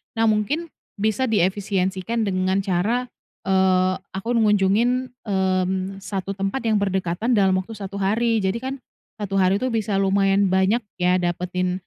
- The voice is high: Yes, high, 195 Hz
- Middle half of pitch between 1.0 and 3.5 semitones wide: Yes, average, 2.7 semitones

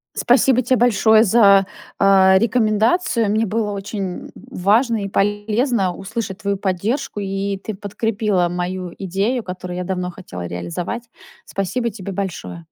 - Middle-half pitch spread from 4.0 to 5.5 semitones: No, average, 3.2 semitones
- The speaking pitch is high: Yes, high, 200 Hz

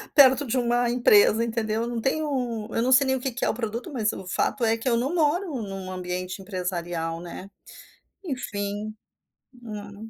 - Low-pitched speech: No, high, 225 Hz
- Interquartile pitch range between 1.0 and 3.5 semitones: No, average, 4.0 semitones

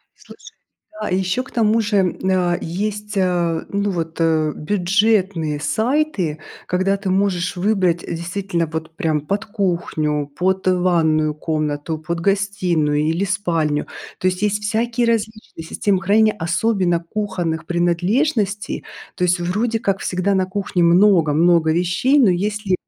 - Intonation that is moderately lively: Yes, average, 3.6 semitones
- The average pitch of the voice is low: No, medium, 185 Hz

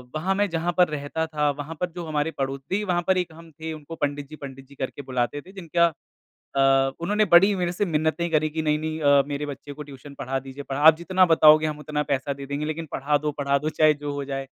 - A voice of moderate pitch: Yes, medium, 150 Hz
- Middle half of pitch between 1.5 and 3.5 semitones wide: Yes, average, 2.7 semitones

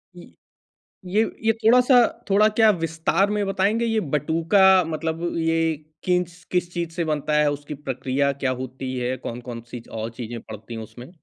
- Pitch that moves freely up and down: Yes, wide, 6.3 semitones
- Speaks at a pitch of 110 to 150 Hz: No, medium, 165 Hz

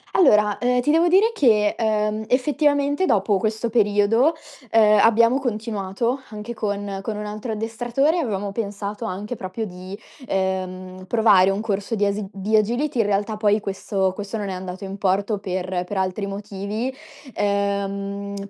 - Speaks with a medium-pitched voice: No, high, 210 Hz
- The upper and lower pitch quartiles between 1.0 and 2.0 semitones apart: No, narrow, 2.6 semitones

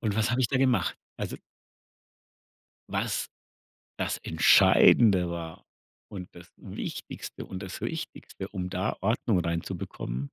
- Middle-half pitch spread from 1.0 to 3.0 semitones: No, average, 4.2 semitones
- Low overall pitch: Yes, very low, 95 Hz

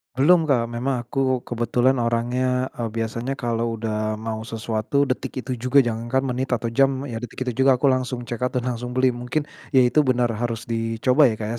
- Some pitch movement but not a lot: No, narrow, 2.1 semitones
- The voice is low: Yes, low, 125 Hz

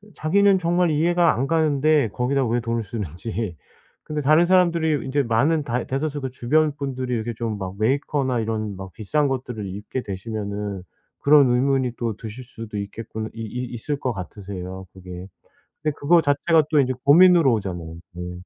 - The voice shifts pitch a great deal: Yes, wide, 5.9 semitones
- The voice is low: Yes, low, 125 Hz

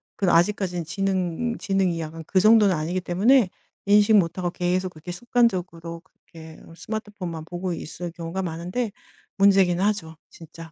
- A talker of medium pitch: Yes, medium, 180 Hz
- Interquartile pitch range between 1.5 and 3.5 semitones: Yes, average, 3.1 semitones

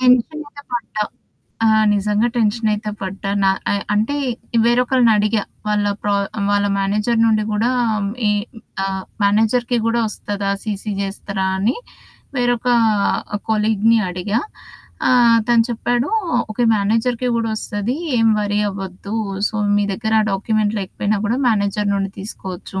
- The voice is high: Yes, high, 215 Hz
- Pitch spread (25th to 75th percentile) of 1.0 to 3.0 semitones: Yes, narrow, 2.6 semitones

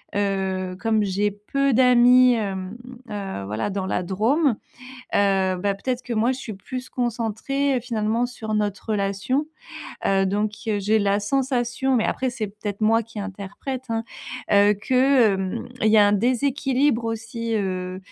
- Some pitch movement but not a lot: Yes, average, 3.7 semitones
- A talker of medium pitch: No, high, 215 Hz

